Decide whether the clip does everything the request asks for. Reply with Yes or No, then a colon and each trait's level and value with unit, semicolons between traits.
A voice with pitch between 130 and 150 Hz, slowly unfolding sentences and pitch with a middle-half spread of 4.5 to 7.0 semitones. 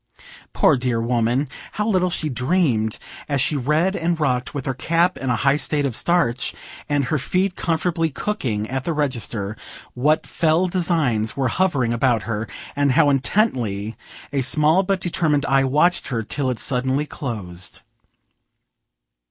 No: medium, 140 Hz; average, 155 wpm; average, 5.2 semitones